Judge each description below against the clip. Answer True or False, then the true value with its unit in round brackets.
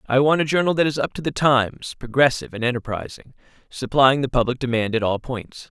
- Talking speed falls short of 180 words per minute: False (205 wpm)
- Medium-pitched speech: False (130 Hz)